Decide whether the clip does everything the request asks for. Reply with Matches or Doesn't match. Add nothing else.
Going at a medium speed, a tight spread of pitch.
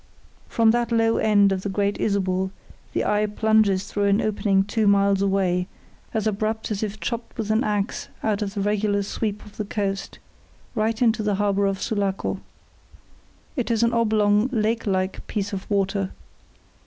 Matches